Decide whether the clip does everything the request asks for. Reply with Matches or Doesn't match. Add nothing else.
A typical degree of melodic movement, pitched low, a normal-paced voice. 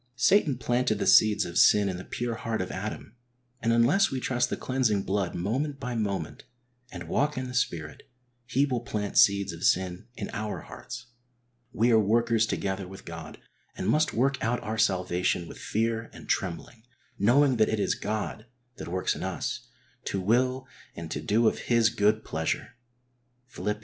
Matches